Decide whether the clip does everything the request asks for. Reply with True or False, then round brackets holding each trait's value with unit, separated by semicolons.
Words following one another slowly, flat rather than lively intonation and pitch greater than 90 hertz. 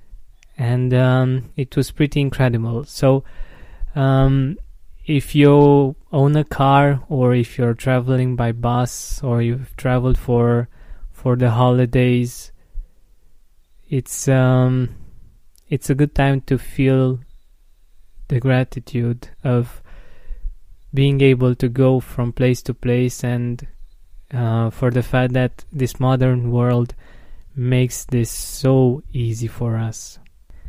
True (115 wpm; 2.2 semitones; 125 Hz)